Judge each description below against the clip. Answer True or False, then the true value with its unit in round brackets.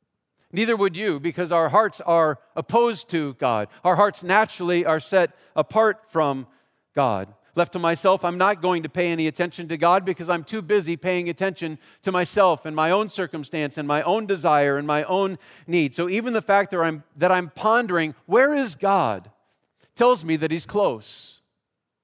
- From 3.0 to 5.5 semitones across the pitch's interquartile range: True (3.8 semitones)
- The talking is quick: False (180 wpm)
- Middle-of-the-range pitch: True (175 Hz)